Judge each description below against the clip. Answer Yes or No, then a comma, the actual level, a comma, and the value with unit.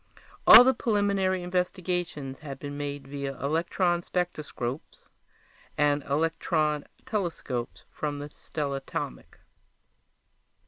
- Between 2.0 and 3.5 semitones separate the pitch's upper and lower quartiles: No, average, 4.0 semitones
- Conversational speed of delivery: No, slow, 80 wpm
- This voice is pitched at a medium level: Yes, medium, 150 Hz